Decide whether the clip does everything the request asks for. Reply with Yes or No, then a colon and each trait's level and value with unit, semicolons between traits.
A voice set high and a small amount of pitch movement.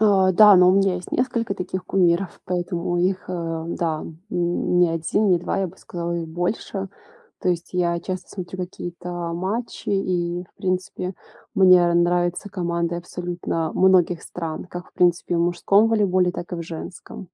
No: medium, 180 Hz; narrow, 1.6 semitones